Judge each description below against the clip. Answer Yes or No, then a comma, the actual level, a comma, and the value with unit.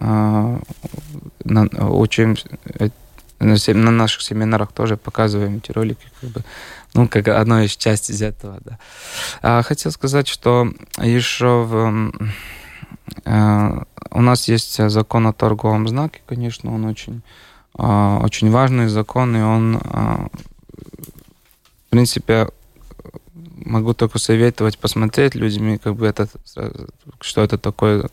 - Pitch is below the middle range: Yes, low, 110 Hz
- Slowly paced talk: No, average, 125 wpm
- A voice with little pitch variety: Yes, narrow, 2.1 semitones